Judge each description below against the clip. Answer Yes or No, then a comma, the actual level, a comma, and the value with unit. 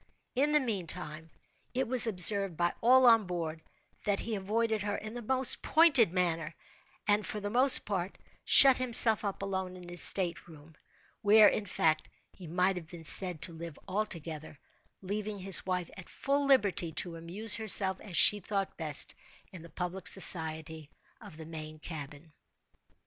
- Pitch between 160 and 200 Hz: Yes, high, 190 Hz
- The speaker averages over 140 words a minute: Yes, average, 165 wpm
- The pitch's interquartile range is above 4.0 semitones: Yes, average, 4.5 semitones